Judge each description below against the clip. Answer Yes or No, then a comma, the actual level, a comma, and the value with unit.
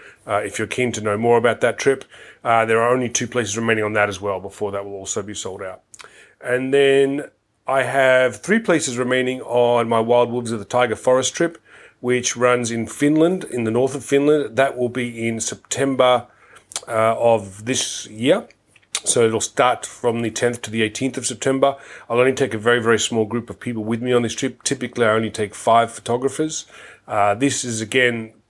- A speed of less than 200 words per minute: No, fast, 205 wpm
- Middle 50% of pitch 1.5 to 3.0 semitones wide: Yes, narrow, 2.5 semitones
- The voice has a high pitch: No, low, 120 Hz